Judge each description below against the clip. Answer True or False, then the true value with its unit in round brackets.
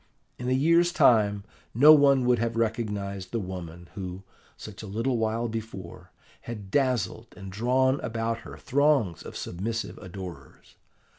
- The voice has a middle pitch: False (115 Hz)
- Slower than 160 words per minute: True (145 wpm)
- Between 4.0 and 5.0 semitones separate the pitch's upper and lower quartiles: True (4.3 semitones)